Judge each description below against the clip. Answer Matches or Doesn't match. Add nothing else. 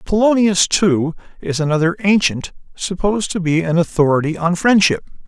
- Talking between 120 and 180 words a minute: Matches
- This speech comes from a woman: Doesn't match